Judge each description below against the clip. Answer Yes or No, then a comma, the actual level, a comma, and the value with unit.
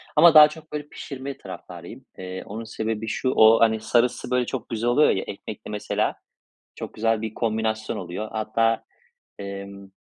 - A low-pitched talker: Yes, low, 110 Hz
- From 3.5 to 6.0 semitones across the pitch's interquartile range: No, average, 2.9 semitones